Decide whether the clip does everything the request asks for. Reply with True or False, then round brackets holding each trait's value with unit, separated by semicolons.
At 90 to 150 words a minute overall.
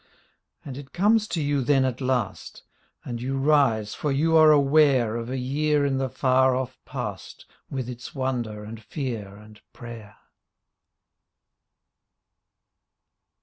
True (140 wpm)